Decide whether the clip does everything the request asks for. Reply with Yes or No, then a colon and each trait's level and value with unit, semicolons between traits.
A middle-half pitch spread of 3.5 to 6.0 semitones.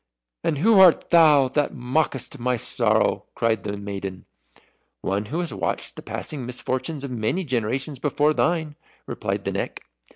Yes: average, 5.0 semitones